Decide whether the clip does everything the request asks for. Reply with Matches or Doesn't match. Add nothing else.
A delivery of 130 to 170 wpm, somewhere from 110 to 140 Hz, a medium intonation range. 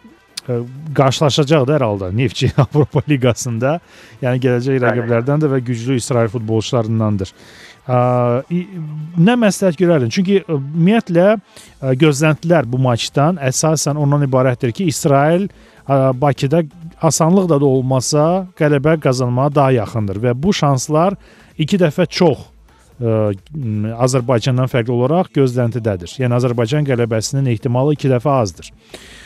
Doesn't match